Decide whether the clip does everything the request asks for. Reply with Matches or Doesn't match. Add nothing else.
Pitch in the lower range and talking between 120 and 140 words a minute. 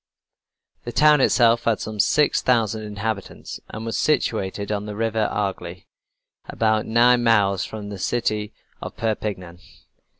Matches